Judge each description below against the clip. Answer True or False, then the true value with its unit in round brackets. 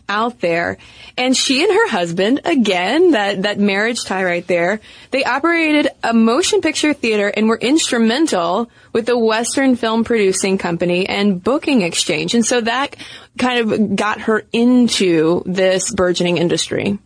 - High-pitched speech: True (225 Hz)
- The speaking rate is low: False (150 wpm)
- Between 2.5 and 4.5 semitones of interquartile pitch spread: False (4.9 semitones)